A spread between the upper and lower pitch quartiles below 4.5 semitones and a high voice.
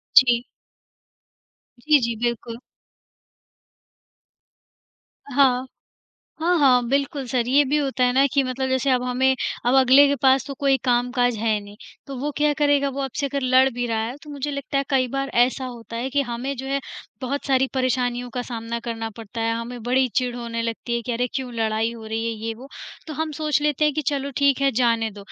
Yes: average, 2.7 semitones; very high, 255 Hz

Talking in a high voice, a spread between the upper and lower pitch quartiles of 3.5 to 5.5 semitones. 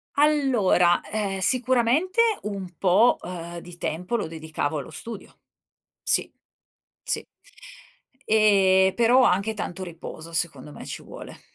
Yes: high, 195 Hz; average, 5.2 semitones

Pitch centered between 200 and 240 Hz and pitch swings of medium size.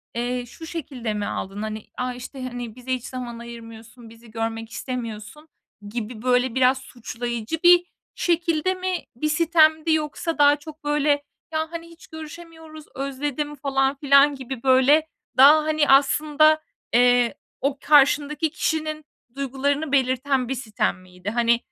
No: very high, 270 Hz; average, 4.2 semitones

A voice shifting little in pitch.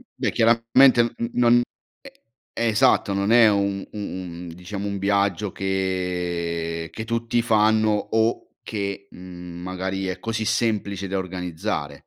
No: average, 3.5 semitones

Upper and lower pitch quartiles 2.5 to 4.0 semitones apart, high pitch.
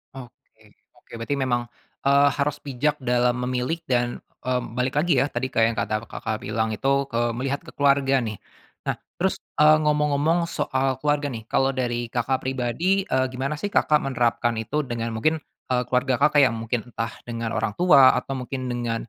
No: average, 3.0 semitones; low, 130 Hz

